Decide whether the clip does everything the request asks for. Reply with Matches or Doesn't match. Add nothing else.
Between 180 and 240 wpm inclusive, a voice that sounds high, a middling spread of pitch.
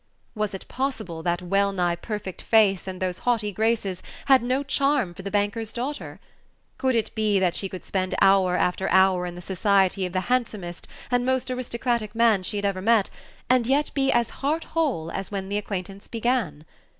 Matches